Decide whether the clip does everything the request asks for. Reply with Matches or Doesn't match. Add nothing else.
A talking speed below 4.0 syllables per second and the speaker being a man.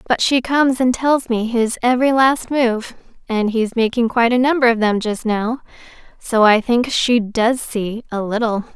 Doesn't match